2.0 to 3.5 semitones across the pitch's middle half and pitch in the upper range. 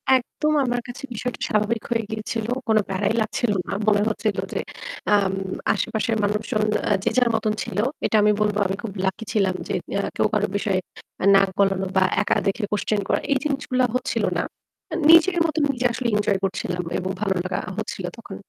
Yes: average, 3.2 semitones; high, 215 Hz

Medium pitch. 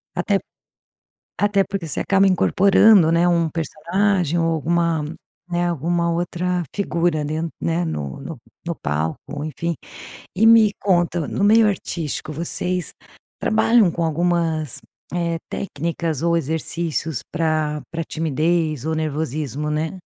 Yes: medium, 170 Hz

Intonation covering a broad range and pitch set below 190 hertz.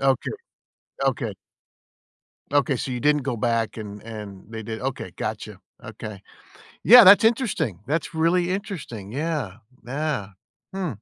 Yes: wide, 7.0 semitones; low, 135 Hz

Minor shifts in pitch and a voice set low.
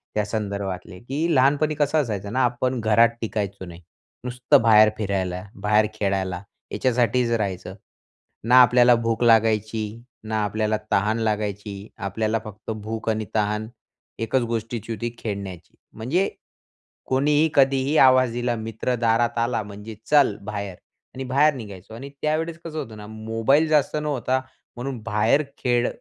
No: average, 3.4 semitones; low, 115 Hz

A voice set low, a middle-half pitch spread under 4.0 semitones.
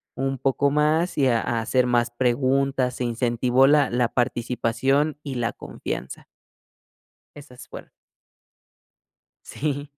Yes: low, 130 Hz; narrow, 2.6 semitones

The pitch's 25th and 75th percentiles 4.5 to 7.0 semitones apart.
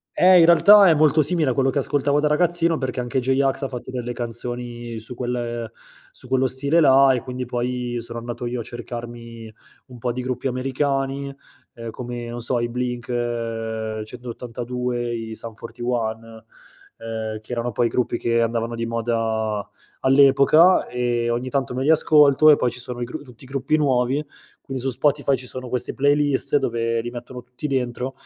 No: narrow, 2.4 semitones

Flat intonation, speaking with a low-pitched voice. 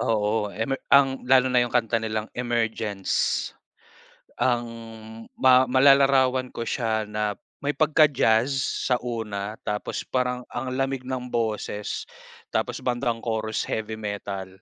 No: average, 3.0 semitones; low, 120 Hz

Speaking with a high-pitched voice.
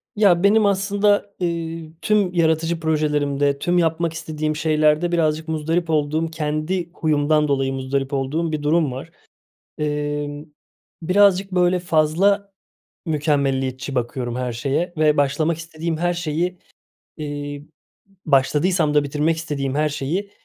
No: medium, 155 Hz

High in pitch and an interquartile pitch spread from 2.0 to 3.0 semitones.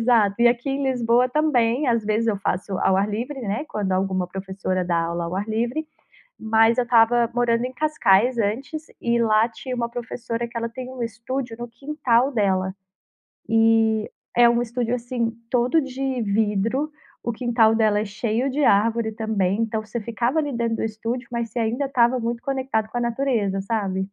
Yes: high, 230 Hz; narrow, 2.5 semitones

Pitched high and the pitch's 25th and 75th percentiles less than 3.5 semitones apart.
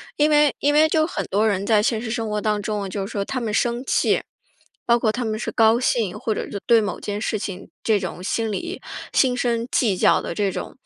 Yes: high, 220 Hz; average, 2.8 semitones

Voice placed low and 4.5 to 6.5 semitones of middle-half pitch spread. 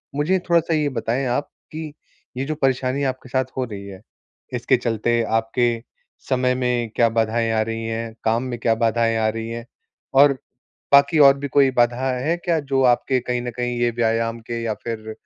No: low, 120 Hz; average, 3.0 semitones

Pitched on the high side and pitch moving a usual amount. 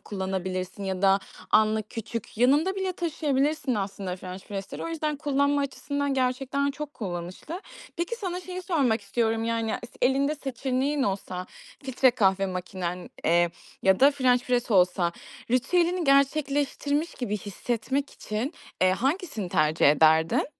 No: very high, 250 Hz; wide, 6.8 semitones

